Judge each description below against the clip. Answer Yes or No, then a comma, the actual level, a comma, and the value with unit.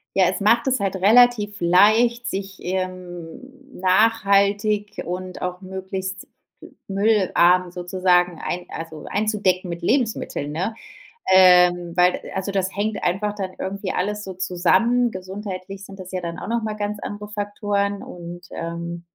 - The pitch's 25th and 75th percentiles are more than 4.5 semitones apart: No, narrow, 2.5 semitones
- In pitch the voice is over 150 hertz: Yes, high, 190 Hz